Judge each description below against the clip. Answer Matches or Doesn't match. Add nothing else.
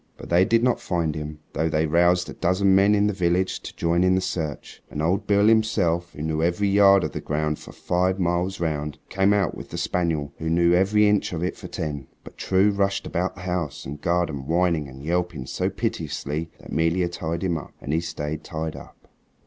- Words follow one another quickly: Matches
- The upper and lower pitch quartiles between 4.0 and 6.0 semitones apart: Doesn't match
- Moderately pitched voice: Doesn't match